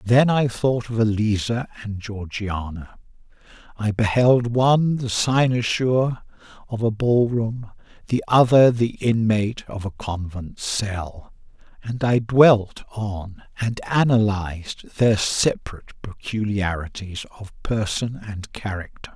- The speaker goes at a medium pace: No, slow, 115 wpm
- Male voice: Yes, male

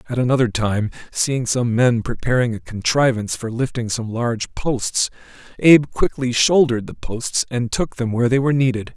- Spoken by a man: Yes, male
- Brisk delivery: No, average, 175 wpm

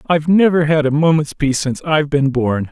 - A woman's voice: No, male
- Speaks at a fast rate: Yes, fast, 220 wpm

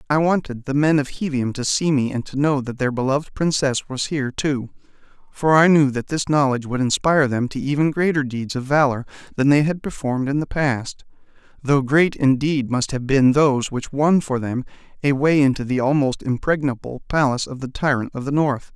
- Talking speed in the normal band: No, fast, 210 wpm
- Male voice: Yes, male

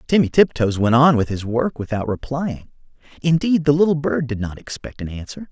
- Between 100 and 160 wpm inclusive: No, average, 195 wpm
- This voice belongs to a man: Yes, male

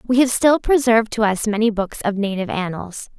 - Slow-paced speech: No, fast, 205 wpm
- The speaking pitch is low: No, high, 220 Hz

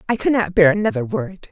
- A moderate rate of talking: No, fast, 240 wpm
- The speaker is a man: No, female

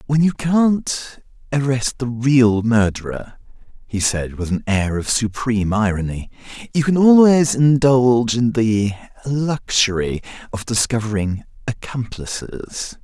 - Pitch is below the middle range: Yes, low, 120 Hz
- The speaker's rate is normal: No, slow, 115 wpm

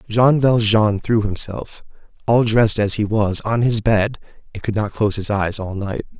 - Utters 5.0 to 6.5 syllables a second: No, 4.7 syllables/s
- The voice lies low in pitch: Yes, low, 110 Hz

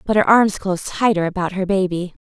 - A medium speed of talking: No, fast, 215 wpm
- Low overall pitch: No, high, 190 Hz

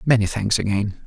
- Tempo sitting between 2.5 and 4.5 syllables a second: No, 5.3 syllables/s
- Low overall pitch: Yes, low, 105 Hz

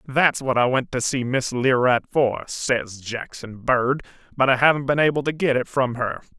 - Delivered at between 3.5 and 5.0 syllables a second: Yes, 4.6 syllables/s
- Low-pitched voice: Yes, low, 130 Hz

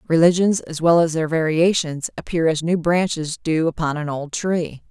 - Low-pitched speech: No, medium, 165 Hz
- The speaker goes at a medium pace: Yes, average, 185 wpm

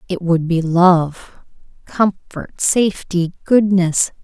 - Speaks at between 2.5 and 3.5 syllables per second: Yes, 3.3 syllables/s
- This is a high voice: No, medium, 180 Hz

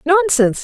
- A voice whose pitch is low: No, very high, 320 Hz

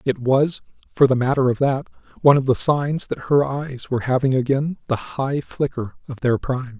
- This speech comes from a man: Yes, male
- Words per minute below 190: No, fast, 205 wpm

